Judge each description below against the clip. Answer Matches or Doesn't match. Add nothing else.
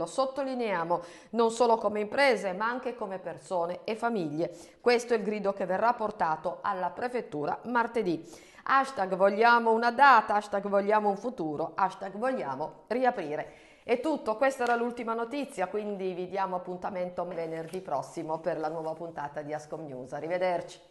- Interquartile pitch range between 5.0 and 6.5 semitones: Matches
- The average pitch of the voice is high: Matches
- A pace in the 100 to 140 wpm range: Doesn't match